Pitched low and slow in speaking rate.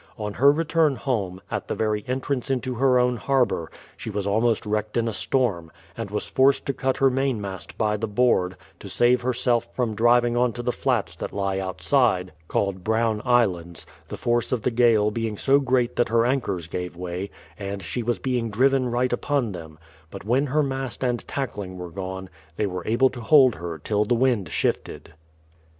No: low, 115 Hz; average, 195 wpm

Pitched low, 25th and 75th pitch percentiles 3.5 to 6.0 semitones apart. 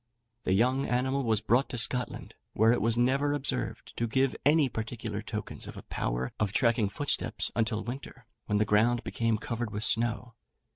No: low, 120 Hz; average, 2.7 semitones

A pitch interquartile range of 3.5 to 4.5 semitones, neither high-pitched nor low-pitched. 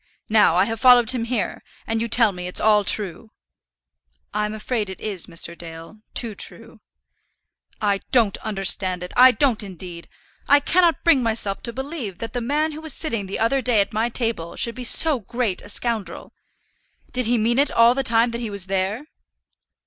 No: average, 4.0 semitones; high, 225 Hz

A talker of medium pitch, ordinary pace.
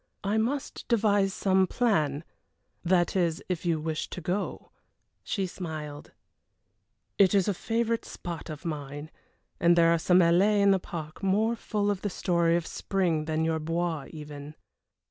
Yes: medium, 175 Hz; average, 160 wpm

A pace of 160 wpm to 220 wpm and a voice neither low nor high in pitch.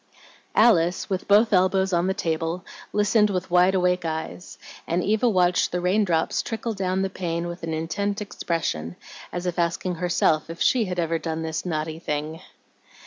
Yes: average, 170 wpm; medium, 180 Hz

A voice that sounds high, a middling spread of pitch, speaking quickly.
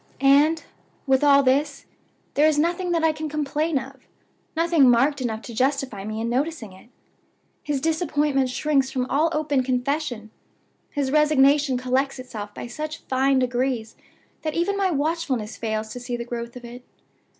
No: very high, 275 Hz; average, 3.6 semitones; average, 160 wpm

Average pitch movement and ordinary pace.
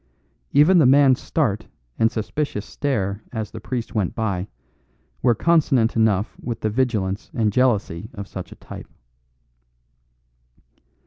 No: average, 4.0 semitones; slow, 130 wpm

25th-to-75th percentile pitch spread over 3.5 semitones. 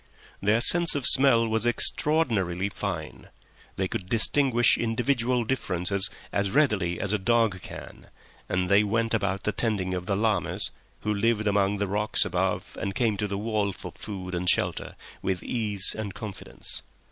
No: average, 3.0 semitones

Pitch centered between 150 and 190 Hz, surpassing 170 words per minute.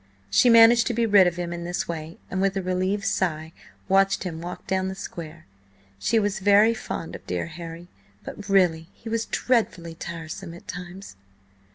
Yes: medium, 185 Hz; average, 185 wpm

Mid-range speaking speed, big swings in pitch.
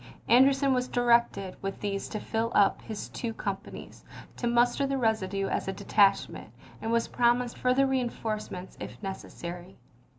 No: average, 160 wpm; average, 3.9 semitones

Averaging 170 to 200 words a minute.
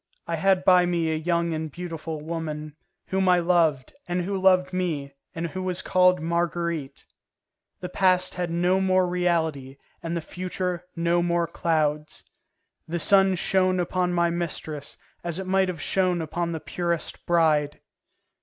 No: average, 155 wpm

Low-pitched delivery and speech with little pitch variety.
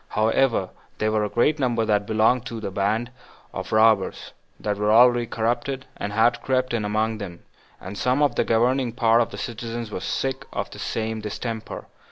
Yes: low, 115 Hz; narrow, 2.2 semitones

